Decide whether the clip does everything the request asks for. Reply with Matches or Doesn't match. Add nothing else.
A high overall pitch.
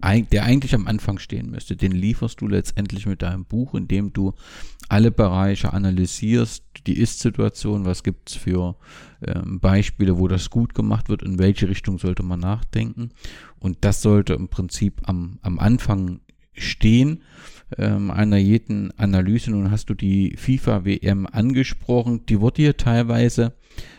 Doesn't match